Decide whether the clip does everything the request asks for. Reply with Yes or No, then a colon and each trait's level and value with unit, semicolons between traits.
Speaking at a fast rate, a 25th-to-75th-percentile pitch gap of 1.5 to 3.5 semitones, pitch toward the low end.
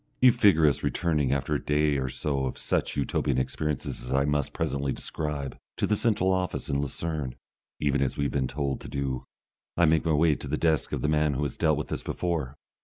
Yes: fast, 225 wpm; narrow, 2.5 semitones; very low, 75 Hz